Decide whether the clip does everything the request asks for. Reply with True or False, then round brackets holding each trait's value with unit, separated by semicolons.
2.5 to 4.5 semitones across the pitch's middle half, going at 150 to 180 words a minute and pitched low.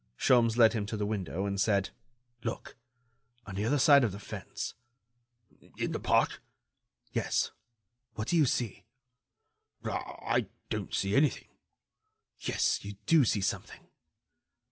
False (3.4 semitones; 135 wpm; 110 Hz)